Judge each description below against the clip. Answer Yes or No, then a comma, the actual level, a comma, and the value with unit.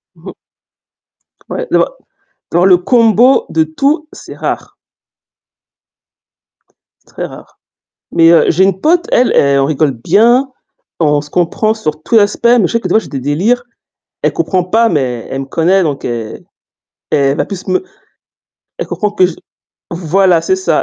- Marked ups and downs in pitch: Yes, wide, 6.9 semitones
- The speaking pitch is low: No, medium, 185 Hz